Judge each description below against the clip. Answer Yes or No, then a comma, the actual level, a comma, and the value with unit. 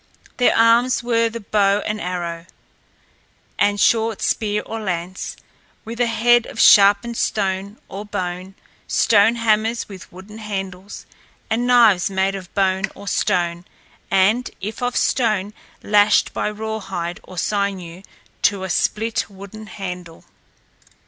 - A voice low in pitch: No, high, 205 Hz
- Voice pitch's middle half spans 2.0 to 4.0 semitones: Yes, average, 2.8 semitones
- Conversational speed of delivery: No, slow, 130 wpm